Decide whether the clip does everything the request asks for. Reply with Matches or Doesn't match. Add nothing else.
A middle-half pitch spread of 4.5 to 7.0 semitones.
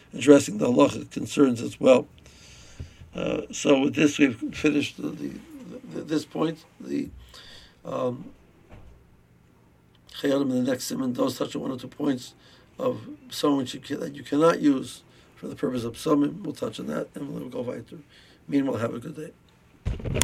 Matches